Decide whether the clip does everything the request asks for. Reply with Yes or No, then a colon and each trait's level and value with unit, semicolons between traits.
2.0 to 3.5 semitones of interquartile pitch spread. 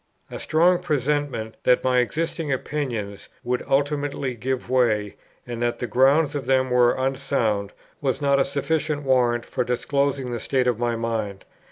Yes: average, 2.9 semitones